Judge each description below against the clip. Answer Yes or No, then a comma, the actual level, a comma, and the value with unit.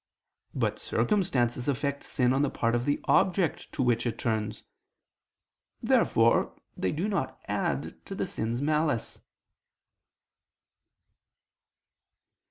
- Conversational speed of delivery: No, slow, 110 wpm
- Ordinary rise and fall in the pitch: Yes, average, 4.2 semitones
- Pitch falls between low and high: No, low, 130 Hz